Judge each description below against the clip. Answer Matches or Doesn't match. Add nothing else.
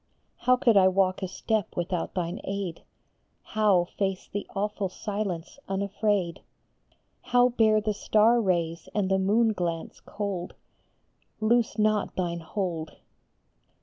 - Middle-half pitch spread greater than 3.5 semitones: Doesn't match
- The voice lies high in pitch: Matches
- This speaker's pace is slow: Matches